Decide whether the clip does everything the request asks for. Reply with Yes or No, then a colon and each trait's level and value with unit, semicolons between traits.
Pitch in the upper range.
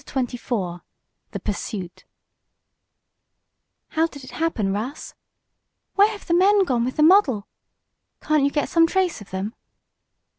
Yes: very high, 275 Hz